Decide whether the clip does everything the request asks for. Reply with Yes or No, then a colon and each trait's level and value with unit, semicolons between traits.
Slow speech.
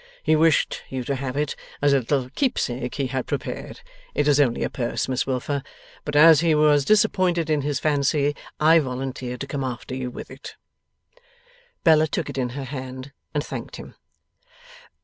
No: average, 180 wpm